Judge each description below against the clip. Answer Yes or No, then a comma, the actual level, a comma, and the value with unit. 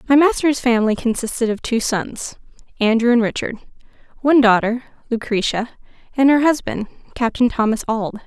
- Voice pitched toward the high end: Yes, high, 240 Hz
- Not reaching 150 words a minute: Yes, average, 140 wpm